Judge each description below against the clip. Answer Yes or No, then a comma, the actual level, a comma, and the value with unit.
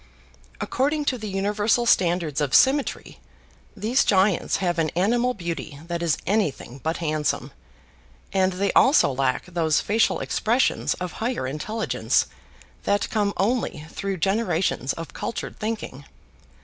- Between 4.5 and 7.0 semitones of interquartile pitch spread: Yes, average, 5.2 semitones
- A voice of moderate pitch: No, high, 195 Hz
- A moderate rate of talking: No, slow, 130 wpm